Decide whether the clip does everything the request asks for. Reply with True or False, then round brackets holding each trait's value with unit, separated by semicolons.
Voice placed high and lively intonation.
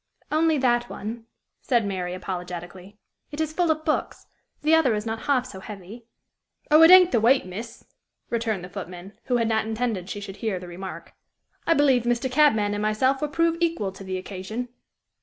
True (225 Hz; 6.1 semitones)